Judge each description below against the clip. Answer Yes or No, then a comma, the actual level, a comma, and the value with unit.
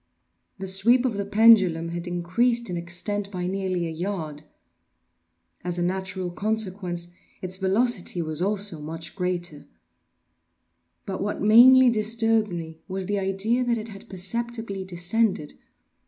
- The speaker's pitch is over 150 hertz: Yes, high, 190 Hz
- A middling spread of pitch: Yes, average, 3.8 semitones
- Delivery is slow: Yes, slow, 130 wpm